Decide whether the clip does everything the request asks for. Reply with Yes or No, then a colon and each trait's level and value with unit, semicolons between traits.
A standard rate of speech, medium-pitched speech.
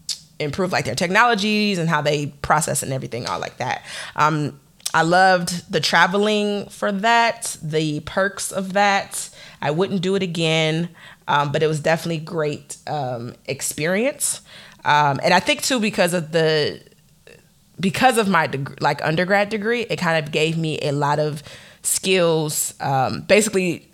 Yes: average, 160 wpm; medium, 165 Hz